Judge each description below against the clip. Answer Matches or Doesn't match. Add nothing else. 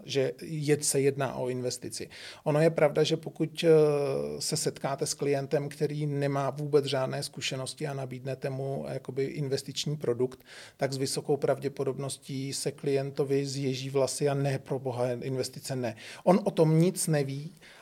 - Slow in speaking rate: Doesn't match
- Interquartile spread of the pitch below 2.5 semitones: Matches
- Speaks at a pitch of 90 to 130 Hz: Doesn't match